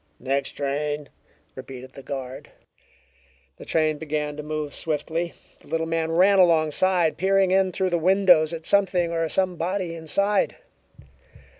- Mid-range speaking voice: Yes, medium, 165 Hz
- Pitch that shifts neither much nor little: Yes, average, 3.6 semitones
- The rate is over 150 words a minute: No, slow, 135 wpm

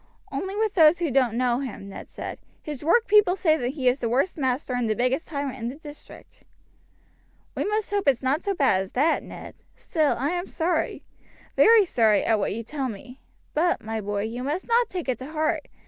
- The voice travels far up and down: Yes, wide, 5.8 semitones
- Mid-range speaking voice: No, very high, 280 Hz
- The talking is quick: Yes, fast, 210 wpm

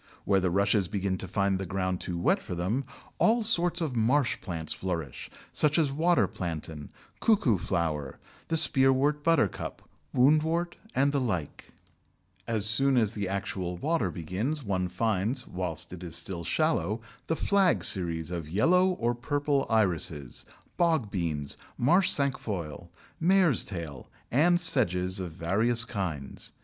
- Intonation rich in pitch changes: Yes, wide, 8.3 semitones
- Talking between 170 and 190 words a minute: No, average, 140 wpm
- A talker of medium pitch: No, low, 105 Hz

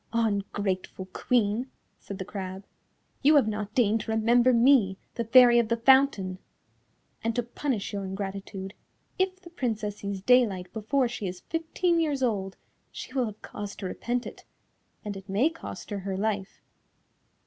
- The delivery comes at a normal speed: Yes, average, 160 wpm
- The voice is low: No, high, 220 Hz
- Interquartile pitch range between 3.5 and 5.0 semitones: Yes, average, 4.2 semitones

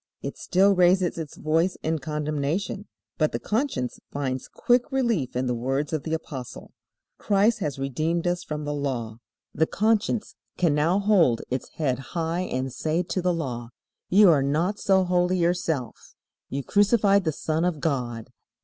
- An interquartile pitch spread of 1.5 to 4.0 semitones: No, average, 5.1 semitones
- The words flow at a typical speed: Yes, average, 165 wpm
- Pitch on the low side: No, medium, 160 Hz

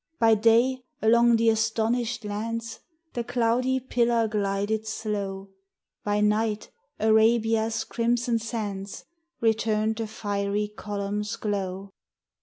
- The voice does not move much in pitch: Yes, narrow, 1.7 semitones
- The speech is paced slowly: Yes, slow, 100 wpm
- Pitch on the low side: No, high, 220 Hz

